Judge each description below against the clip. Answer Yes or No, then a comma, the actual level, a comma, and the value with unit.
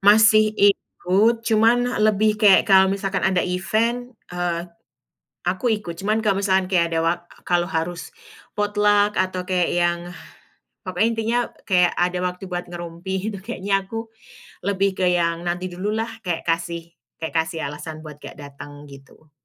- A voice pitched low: No, medium, 185 Hz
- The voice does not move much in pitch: No, average, 3.3 semitones